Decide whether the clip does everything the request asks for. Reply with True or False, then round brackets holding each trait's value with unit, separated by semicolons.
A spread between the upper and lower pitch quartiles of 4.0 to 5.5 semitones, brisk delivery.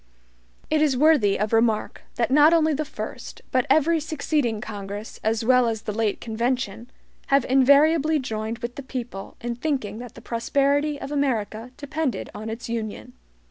False (4.5 semitones; 165 wpm)